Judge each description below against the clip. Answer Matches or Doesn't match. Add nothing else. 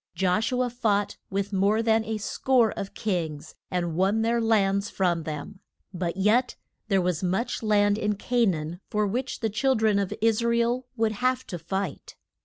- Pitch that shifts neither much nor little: Matches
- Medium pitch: Doesn't match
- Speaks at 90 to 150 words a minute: Doesn't match